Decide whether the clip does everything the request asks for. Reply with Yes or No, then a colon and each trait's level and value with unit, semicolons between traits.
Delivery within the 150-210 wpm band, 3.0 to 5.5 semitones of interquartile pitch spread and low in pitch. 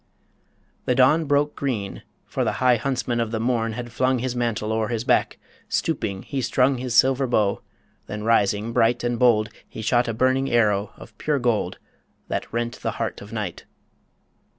No: average, 175 wpm; narrow, 2.6 semitones; low, 120 Hz